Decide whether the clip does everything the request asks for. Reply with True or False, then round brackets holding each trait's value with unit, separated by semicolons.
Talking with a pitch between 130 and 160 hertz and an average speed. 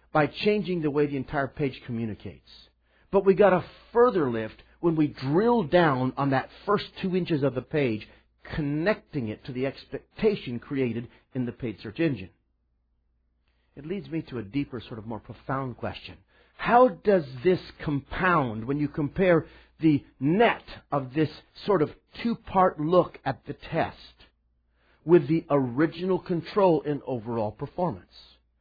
True (140 Hz; 155 wpm)